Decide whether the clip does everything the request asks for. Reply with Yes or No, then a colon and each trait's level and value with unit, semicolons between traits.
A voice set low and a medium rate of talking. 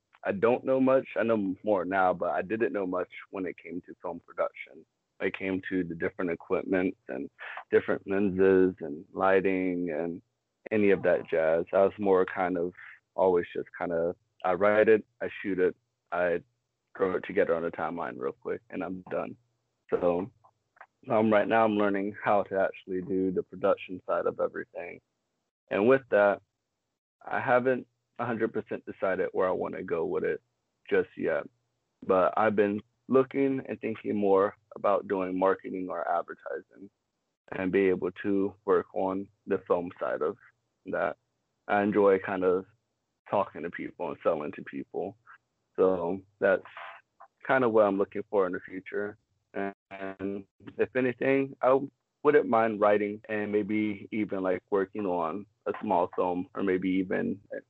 Yes: low, 105 Hz; average, 165 wpm